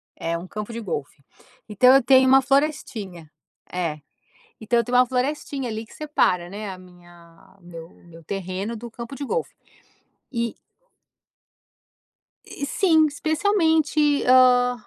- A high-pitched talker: Yes, high, 235 Hz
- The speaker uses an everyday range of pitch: No, wide, 7.2 semitones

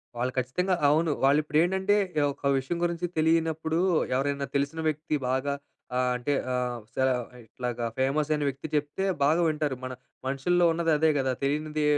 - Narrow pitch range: No, average, 3.4 semitones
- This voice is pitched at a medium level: Yes, medium, 150 Hz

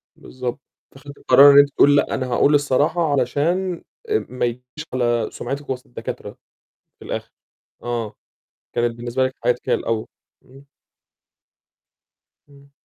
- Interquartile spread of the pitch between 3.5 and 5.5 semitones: No, average, 2.8 semitones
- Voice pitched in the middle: No, low, 130 Hz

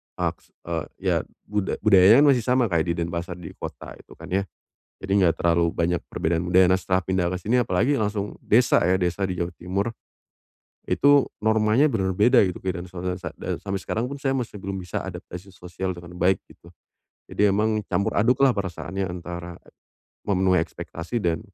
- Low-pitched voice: Yes, very low, 95 Hz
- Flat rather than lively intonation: No, average, 3.4 semitones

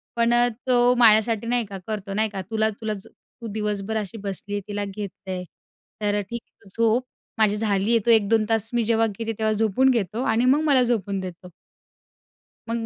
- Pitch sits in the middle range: No, high, 220 Hz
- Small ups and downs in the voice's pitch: Yes, narrow, 2.3 semitones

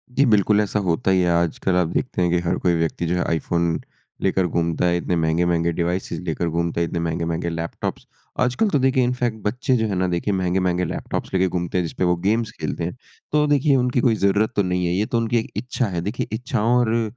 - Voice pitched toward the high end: No, very low, 90 Hz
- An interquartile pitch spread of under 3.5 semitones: No, average, 5.0 semitones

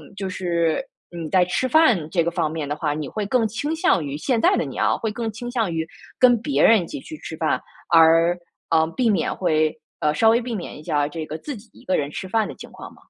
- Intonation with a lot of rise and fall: Yes, wide, 6.4 semitones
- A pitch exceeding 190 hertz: No, medium, 185 Hz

